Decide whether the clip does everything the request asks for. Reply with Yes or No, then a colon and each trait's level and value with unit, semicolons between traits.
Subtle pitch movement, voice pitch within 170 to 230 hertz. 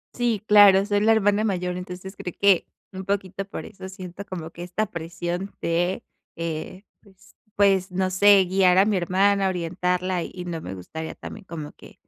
Yes: narrow, 2.1 semitones; medium, 185 Hz